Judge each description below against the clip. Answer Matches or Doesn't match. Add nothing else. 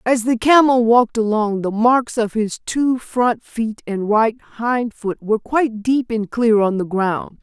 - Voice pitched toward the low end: Doesn't match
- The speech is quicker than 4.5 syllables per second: Doesn't match